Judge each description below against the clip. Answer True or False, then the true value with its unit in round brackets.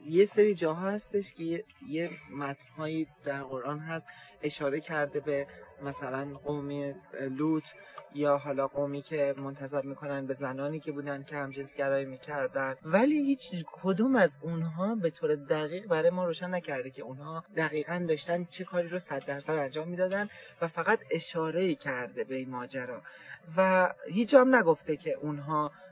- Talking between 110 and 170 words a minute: True (155 wpm)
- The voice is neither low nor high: True (155 Hz)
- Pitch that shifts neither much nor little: True (3.9 semitones)